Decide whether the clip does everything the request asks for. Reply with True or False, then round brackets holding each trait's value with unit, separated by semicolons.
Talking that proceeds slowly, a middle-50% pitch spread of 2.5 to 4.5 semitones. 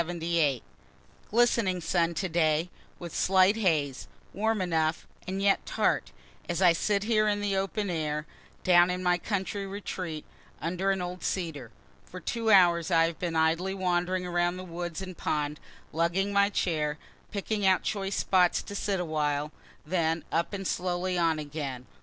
False (155 wpm; 3.0 semitones)